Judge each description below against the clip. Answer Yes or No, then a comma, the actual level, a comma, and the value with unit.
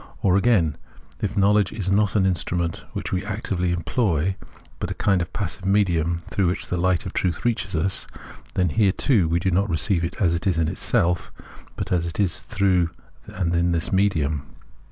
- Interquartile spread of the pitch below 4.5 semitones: Yes, average, 2.8 semitones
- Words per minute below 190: No, average, 195 wpm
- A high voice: No, very low, 90 Hz